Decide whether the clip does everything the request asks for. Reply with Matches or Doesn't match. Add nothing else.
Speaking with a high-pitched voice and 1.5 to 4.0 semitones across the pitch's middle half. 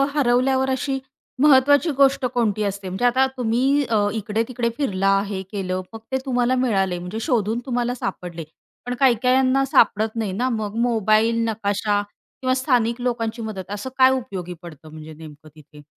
Doesn't match